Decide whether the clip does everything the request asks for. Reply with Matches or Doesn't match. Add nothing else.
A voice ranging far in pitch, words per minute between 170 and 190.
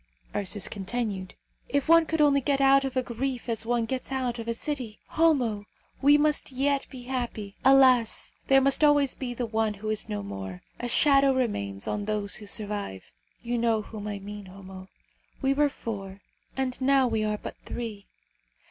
Doesn't match